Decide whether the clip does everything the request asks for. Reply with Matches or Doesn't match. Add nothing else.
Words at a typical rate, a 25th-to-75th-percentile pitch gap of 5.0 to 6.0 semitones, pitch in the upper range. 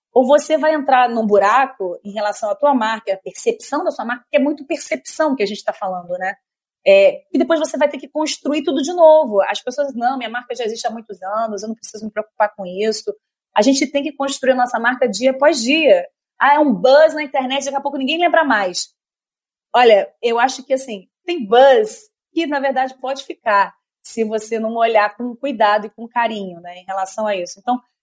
Doesn't match